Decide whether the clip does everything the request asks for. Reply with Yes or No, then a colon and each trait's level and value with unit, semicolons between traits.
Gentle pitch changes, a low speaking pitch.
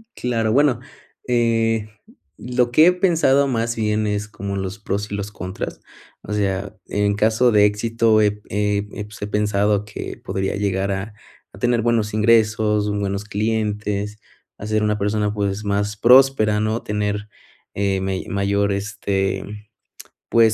Yes: narrow, 1.8 semitones; low, 105 Hz